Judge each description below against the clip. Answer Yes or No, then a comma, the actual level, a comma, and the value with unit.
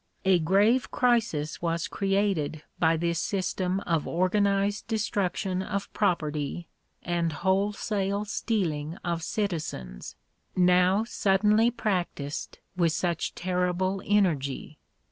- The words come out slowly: Yes, slow, 100 wpm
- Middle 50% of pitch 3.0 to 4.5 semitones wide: Yes, average, 3.3 semitones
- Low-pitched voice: No, medium, 185 Hz